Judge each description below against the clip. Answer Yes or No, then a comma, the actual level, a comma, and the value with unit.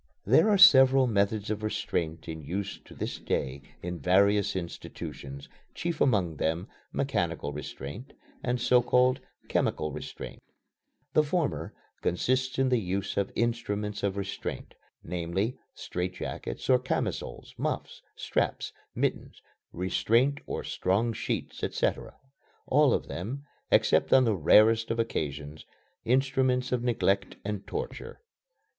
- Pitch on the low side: Yes, low, 105 Hz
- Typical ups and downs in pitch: No, wide, 6.0 semitones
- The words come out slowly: Yes, slow, 125 wpm